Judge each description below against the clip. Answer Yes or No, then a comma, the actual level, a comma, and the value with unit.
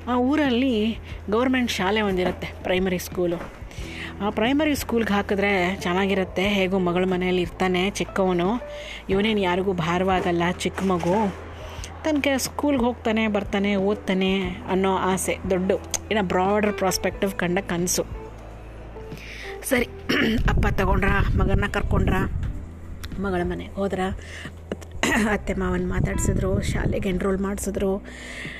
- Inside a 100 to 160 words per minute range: Yes, fast, 105 wpm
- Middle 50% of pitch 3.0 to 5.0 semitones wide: No, narrow, 2.6 semitones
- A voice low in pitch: No, high, 190 Hz